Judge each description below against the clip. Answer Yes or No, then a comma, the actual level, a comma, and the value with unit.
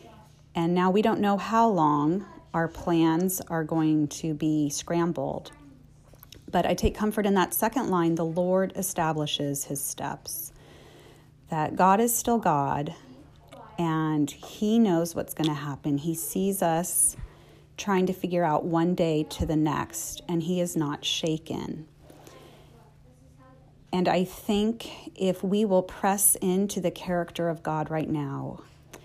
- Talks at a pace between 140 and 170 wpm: Yes, average, 145 wpm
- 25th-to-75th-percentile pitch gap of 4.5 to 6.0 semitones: No, average, 3.6 semitones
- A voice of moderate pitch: Yes, medium, 170 Hz